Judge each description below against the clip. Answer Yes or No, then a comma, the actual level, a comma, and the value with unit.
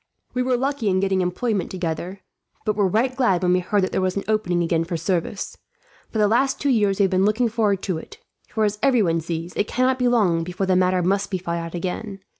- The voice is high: Yes, high, 195 Hz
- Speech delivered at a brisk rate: Yes, fast, 240 wpm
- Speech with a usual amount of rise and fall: Yes, average, 3.5 semitones